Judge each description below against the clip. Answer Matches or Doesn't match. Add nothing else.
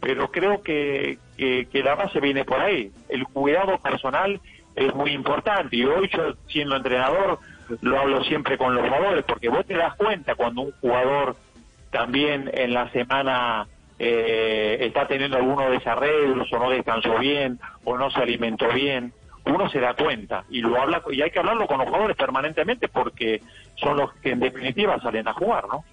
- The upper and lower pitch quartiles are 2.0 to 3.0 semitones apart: Matches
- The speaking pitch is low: Matches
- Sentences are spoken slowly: Doesn't match